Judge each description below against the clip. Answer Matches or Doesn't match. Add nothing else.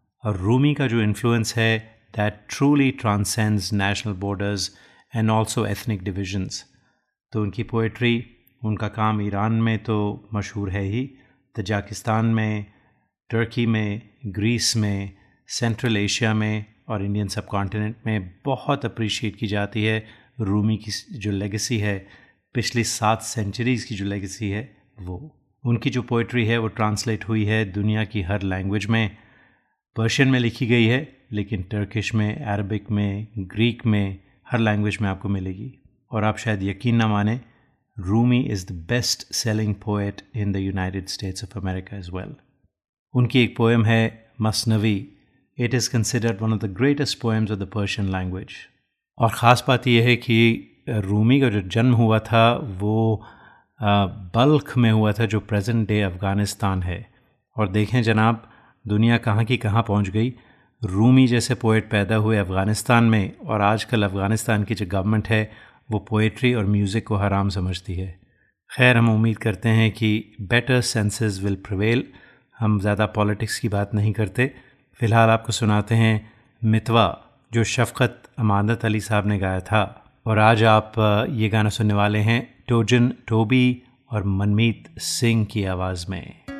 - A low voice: Matches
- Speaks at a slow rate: Doesn't match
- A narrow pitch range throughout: Matches